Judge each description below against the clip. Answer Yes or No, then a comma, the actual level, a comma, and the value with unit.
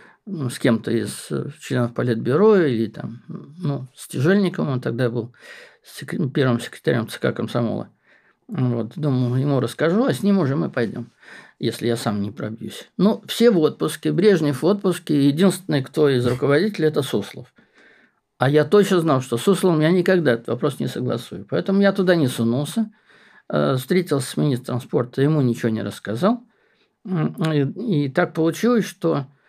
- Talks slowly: No, average, 155 wpm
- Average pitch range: No, wide, 6.9 semitones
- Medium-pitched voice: Yes, medium, 145 Hz